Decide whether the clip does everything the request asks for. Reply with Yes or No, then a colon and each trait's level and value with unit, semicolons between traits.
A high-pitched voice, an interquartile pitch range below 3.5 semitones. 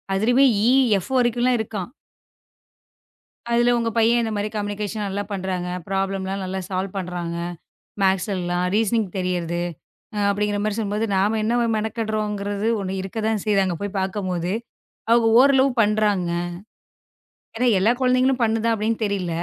Yes: high, 205 Hz; average, 2.9 semitones